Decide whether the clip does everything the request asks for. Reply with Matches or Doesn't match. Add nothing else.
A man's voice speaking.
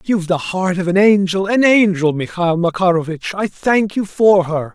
Matches